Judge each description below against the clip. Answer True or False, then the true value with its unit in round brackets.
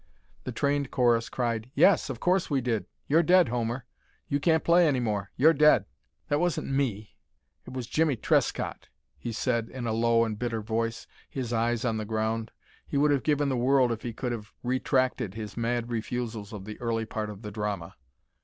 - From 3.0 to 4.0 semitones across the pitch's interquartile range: True (3.5 semitones)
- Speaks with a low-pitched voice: True (120 Hz)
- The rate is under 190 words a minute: False (195 wpm)